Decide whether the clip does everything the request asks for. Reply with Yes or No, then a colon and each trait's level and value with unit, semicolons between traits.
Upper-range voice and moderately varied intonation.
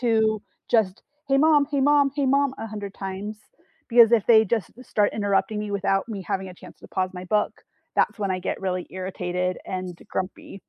Yes: high, 205 Hz; average, 3.8 semitones